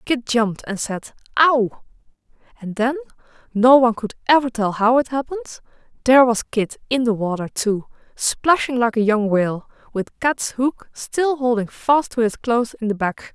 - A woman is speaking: Yes, female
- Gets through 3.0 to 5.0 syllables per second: Yes, 4.8 syllables/s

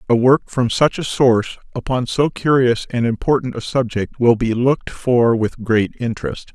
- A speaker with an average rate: Yes, average, 185 wpm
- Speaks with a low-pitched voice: Yes, low, 125 Hz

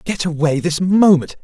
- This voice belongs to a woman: No, male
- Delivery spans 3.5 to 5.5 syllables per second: Yes, 4.6 syllables/s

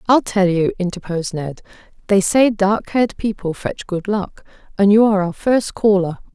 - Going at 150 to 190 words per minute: Yes, average, 180 wpm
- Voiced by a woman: Yes, female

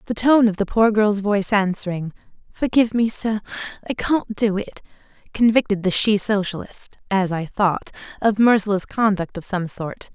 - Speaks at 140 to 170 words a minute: Yes, average, 155 wpm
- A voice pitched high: Yes, high, 205 Hz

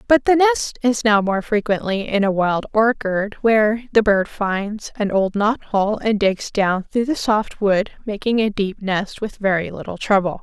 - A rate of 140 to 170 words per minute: No, average, 195 wpm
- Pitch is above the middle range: Yes, high, 210 Hz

